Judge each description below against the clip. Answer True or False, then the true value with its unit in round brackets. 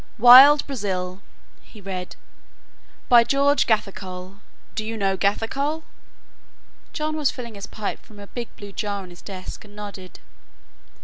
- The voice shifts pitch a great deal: False (4.2 semitones)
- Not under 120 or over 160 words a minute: True (140 wpm)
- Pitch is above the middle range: True (210 Hz)